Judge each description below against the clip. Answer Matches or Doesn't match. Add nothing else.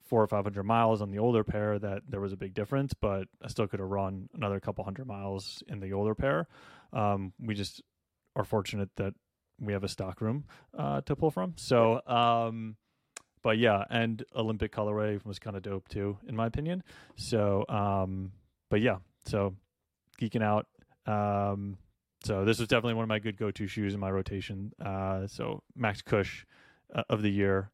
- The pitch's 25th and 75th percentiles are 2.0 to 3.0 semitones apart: Matches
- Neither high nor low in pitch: Doesn't match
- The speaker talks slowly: Doesn't match